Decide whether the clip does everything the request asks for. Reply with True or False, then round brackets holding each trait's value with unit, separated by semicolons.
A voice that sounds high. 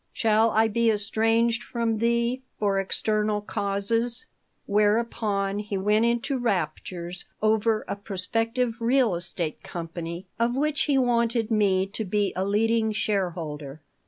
True (215 Hz)